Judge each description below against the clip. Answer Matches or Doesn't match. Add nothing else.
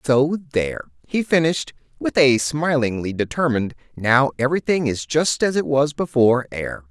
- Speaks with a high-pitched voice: Doesn't match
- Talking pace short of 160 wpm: Matches